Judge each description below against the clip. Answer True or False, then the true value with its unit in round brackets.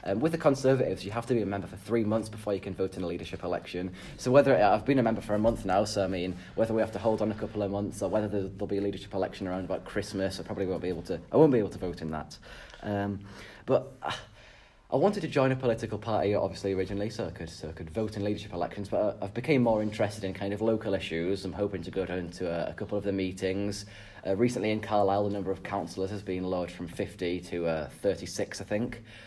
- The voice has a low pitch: True (100 Hz)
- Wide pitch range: False (2.4 semitones)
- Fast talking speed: True (265 wpm)